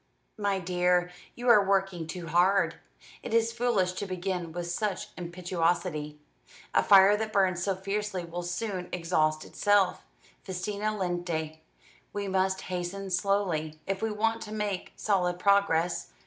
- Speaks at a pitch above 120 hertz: Yes, medium, 185 Hz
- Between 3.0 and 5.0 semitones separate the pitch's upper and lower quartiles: No, narrow, 2.5 semitones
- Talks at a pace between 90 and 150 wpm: Yes, average, 140 wpm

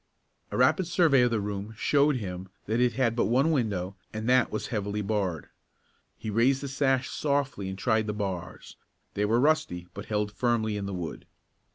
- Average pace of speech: Yes, average, 190 wpm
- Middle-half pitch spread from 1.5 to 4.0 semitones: No, average, 4.5 semitones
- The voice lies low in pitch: Yes, low, 110 Hz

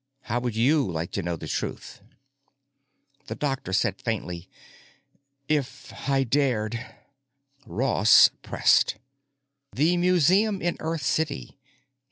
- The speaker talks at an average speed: No, slow, 110 wpm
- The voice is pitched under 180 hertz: Yes, low, 135 Hz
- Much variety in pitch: Yes, wide, 6.5 semitones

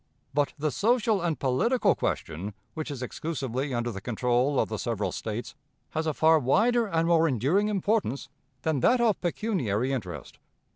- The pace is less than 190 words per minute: Yes, average, 160 wpm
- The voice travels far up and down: Yes, wide, 7.3 semitones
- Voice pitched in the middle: Yes, medium, 145 Hz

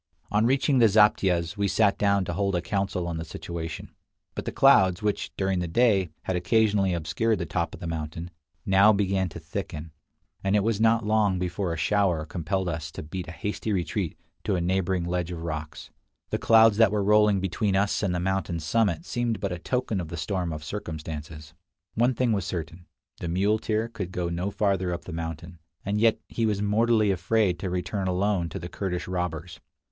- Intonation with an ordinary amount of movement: Yes, average, 3.4 semitones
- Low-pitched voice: Yes, very low, 95 Hz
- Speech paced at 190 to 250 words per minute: Yes, average, 200 wpm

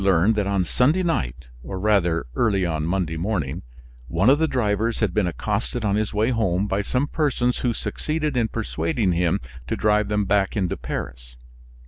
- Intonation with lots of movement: No, average, 4.6 semitones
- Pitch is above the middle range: No, low, 105 Hz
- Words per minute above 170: Yes, average, 190 wpm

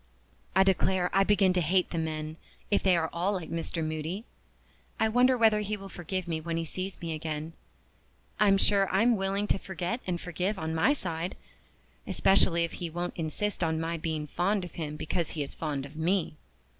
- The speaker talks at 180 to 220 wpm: Yes, average, 195 wpm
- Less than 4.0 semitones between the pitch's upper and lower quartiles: Yes, average, 3.3 semitones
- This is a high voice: No, medium, 175 Hz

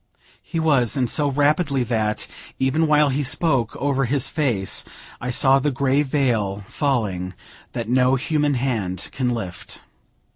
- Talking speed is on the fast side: No, average, 145 wpm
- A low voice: Yes, low, 130 Hz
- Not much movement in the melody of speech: No, average, 3.7 semitones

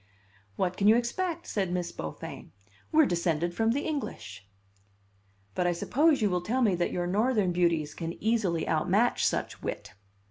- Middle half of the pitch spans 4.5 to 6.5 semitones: Yes, wide, 5.5 semitones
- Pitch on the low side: No, medium, 185 Hz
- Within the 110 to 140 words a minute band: No, average, 165 wpm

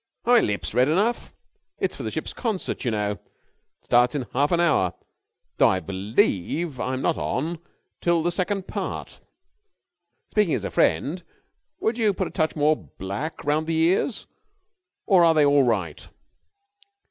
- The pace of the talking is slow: No, average, 165 wpm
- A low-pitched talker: No, medium, 155 Hz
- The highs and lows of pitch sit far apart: Yes, wide, 6.3 semitones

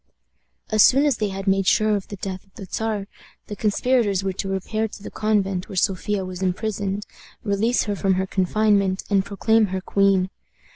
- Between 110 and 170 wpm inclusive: No, average, 190 wpm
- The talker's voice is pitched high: Yes, high, 200 Hz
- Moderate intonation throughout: No, narrow, 2.1 semitones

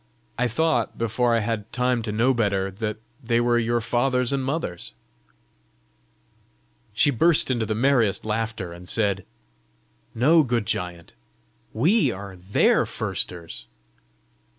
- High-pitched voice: No, low, 115 Hz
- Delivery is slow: Yes, slow, 130 wpm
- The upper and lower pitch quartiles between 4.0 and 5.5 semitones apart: No, average, 3.5 semitones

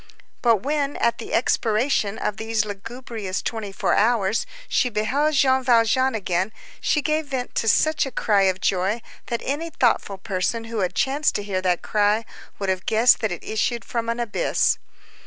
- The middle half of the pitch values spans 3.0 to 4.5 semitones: Yes, average, 4.1 semitones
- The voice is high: Yes, high, 225 Hz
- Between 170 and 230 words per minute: Yes, average, 175 wpm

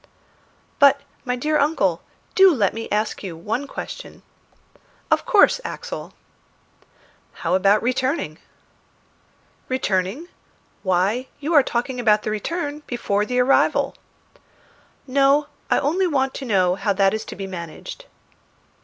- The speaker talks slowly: Yes, slow, 125 wpm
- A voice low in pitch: No, high, 245 Hz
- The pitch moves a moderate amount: No, wide, 6.0 semitones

